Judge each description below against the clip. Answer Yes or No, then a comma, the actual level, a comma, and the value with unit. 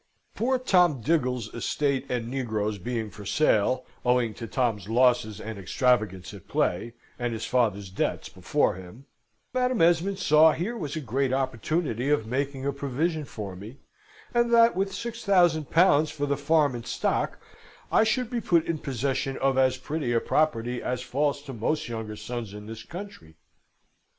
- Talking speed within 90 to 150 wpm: No, average, 170 wpm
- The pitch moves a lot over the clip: Yes, wide, 5.7 semitones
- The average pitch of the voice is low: Yes, low, 130 Hz